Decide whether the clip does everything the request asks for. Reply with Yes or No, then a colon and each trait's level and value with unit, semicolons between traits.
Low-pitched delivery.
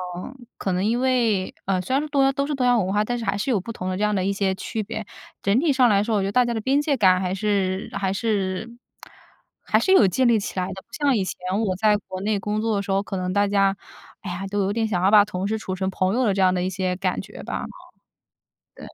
No: high, 205 Hz